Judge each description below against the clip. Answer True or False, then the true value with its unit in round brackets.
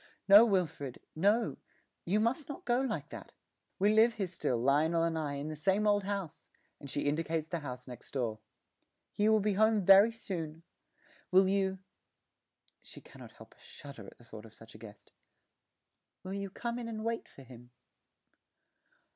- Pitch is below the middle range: False (185 Hz)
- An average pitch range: False (6.7 semitones)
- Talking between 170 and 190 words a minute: True (180 wpm)